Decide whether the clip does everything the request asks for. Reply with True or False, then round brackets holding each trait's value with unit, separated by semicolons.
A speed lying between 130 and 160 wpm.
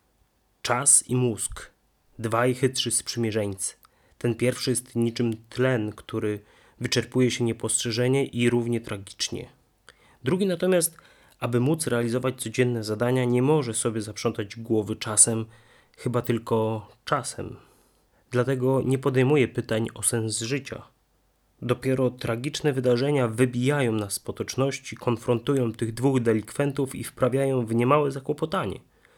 False (120 wpm)